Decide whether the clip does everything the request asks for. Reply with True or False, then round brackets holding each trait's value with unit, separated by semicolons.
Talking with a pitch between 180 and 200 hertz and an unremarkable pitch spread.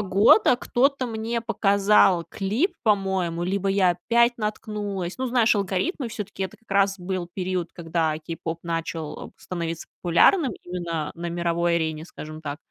True (190 Hz; 4.0 semitones)